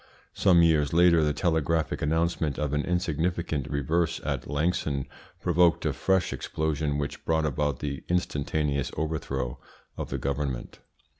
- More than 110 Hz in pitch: No, very low, 75 Hz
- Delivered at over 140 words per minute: No, slow, 135 wpm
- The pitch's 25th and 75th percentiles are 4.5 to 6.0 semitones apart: No, average, 2.7 semitones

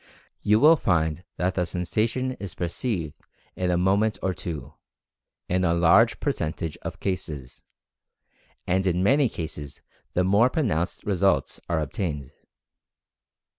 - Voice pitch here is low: Yes, very low, 90 Hz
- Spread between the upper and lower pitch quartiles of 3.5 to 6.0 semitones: Yes, average, 3.9 semitones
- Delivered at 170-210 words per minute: No, slow, 135 wpm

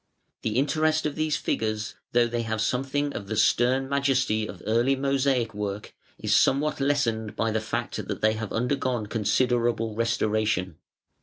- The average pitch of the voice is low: Yes, low, 120 Hz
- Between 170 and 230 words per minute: No, average, 155 wpm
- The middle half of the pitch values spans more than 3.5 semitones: Yes, average, 3.9 semitones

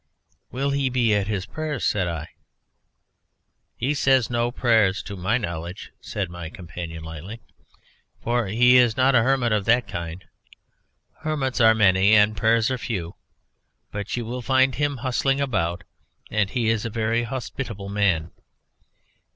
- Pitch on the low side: Yes, low, 110 Hz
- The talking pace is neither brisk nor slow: Yes, average, 150 wpm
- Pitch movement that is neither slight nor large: Yes, average, 4.9 semitones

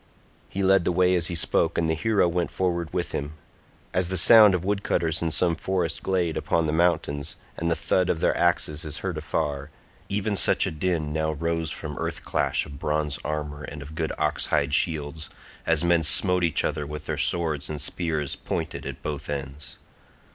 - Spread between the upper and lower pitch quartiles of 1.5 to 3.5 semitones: Yes, average, 2.8 semitones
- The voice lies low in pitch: Yes, very low, 80 Hz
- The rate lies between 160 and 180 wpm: No, average, 190 wpm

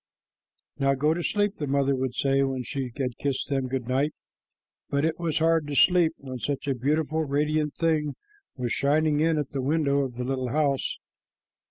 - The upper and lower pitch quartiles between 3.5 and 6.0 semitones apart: No, average, 2.7 semitones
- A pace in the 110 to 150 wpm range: No, average, 200 wpm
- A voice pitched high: No, medium, 140 Hz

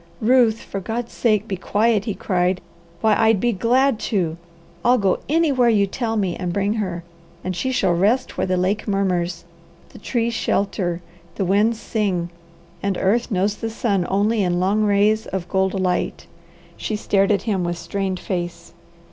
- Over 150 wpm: Yes, average, 175 wpm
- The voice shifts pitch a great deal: No, average, 3.3 semitones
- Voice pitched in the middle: No, high, 200 Hz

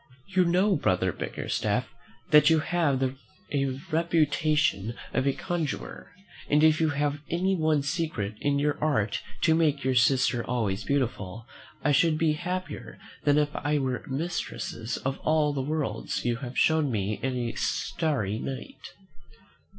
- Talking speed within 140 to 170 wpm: Yes, average, 150 wpm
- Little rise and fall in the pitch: No, average, 3.7 semitones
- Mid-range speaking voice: Yes, medium, 145 Hz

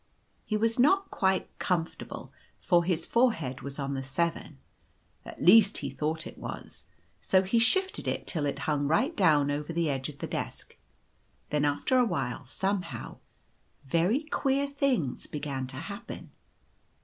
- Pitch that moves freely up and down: Yes, wide, 7.8 semitones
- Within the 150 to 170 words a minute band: Yes, average, 155 wpm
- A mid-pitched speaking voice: Yes, medium, 165 Hz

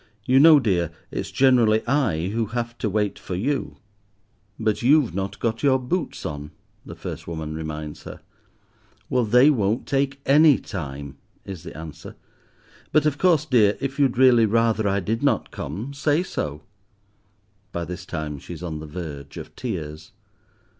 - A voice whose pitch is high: No, low, 110 Hz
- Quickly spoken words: No, average, 165 wpm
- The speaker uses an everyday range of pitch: No, wide, 8.4 semitones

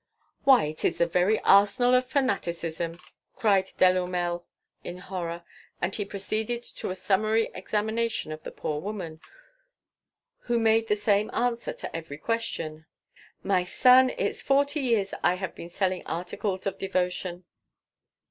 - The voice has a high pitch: Yes, high, 195 Hz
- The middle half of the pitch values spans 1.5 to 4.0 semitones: No, average, 4.4 semitones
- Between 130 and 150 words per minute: Yes, average, 140 wpm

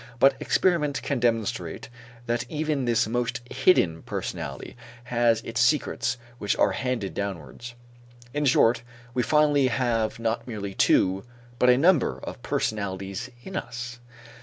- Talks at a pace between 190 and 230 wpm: No, slow, 135 wpm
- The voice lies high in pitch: No, low, 120 Hz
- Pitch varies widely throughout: No, average, 3.3 semitones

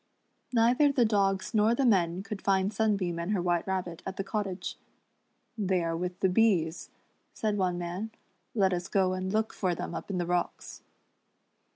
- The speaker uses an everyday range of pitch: Yes, average, 3.1 semitones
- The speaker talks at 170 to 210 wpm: Yes, average, 180 wpm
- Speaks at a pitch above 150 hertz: Yes, high, 190 Hz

